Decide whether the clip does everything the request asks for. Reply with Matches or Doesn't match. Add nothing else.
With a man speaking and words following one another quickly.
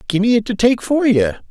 Matches